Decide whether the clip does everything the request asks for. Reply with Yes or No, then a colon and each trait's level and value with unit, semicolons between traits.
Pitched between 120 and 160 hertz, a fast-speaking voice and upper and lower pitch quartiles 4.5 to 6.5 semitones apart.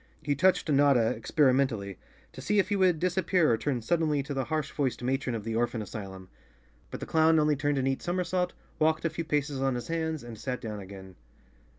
Yes: medium, 140 Hz; fast, 210 wpm; average, 5.1 semitones